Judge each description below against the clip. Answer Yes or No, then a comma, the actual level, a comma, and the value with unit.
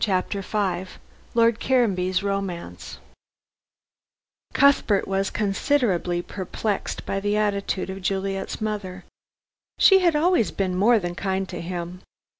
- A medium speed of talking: No, slow, 115 wpm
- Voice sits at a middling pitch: No, high, 195 Hz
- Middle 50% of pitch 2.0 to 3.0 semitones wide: Yes, narrow, 2.6 semitones